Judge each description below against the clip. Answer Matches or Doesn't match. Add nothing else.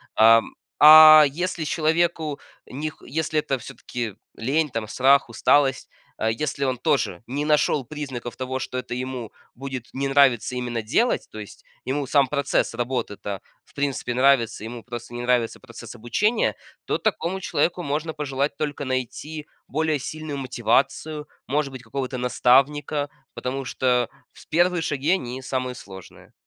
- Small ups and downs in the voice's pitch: Doesn't match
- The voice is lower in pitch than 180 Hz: Matches